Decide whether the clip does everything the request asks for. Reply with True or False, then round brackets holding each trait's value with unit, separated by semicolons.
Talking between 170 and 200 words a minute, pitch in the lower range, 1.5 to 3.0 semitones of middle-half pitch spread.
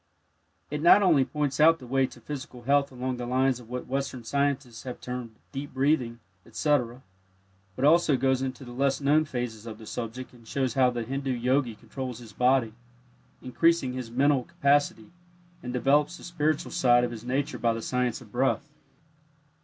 True (180 wpm; 130 Hz; 2.5 semitones)